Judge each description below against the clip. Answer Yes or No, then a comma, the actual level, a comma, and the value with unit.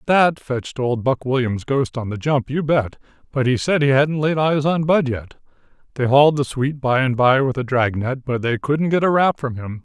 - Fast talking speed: Yes, fast, 245 wpm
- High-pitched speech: No, low, 135 Hz